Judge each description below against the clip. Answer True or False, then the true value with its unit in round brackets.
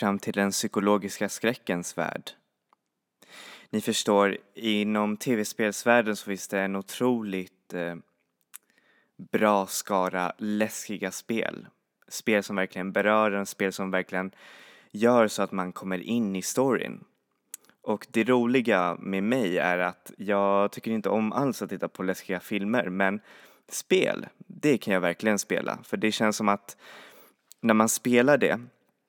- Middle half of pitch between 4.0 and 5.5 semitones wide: False (2.6 semitones)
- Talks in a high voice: False (105 Hz)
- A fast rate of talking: False (140 wpm)